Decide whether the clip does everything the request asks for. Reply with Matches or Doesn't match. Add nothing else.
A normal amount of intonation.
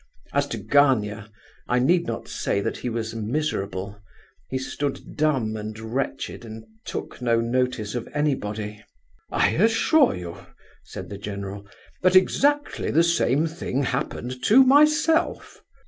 Doesn't match